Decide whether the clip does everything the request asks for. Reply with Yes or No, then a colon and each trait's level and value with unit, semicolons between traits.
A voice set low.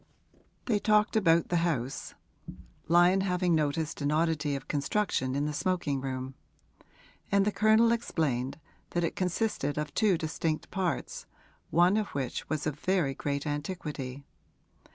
No: medium, 160 Hz